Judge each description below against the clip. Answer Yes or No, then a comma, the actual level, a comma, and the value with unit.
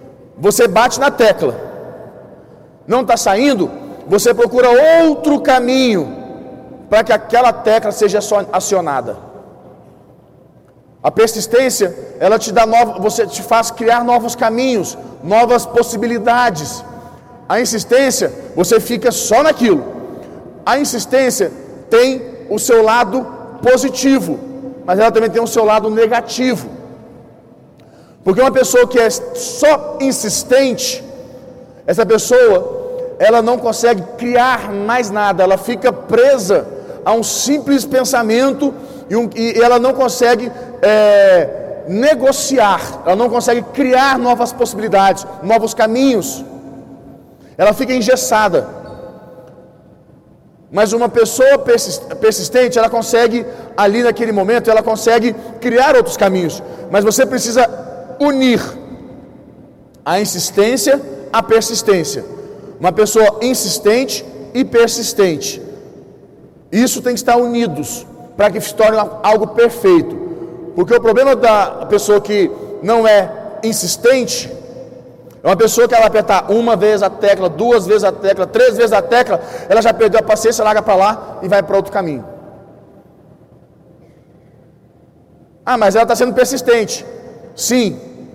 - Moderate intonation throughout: Yes, average, 3.1 semitones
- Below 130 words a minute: Yes, slow, 120 wpm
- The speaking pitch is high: Yes, high, 235 Hz